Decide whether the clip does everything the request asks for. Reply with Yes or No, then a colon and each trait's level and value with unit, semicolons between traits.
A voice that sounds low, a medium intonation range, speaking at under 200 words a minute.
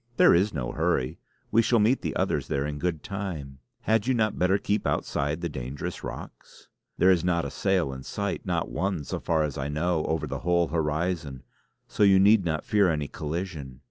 No: very low, 85 Hz; average, 4.7 semitones; fast, 205 wpm